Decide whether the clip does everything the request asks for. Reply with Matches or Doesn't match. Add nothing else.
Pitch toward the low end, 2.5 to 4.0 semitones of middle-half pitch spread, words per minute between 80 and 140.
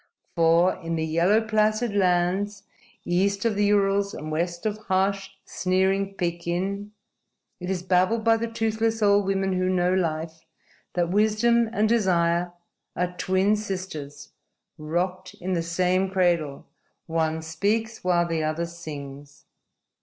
Doesn't match